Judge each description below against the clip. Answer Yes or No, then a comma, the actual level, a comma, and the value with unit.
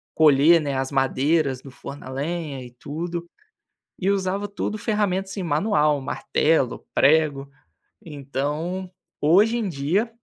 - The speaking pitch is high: No, medium, 155 Hz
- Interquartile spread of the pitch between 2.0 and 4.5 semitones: No, average, 5.1 semitones